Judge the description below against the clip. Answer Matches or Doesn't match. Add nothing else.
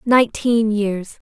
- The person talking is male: Doesn't match